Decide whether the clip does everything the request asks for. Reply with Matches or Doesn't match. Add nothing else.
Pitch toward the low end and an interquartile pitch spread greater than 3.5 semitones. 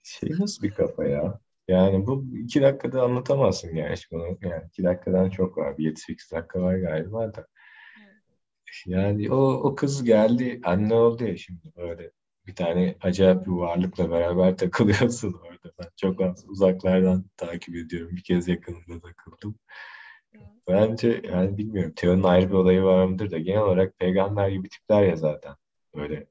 Doesn't match